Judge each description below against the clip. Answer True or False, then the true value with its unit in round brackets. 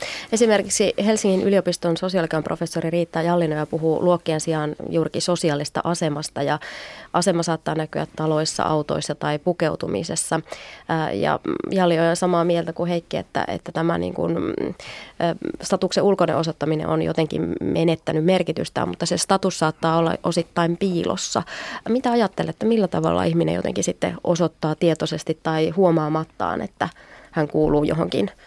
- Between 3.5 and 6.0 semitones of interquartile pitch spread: False (2.4 semitones)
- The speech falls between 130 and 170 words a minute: True (135 wpm)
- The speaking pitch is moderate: True (170 Hz)